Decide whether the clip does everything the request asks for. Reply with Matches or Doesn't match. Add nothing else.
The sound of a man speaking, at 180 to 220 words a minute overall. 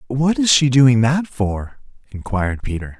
Doesn't match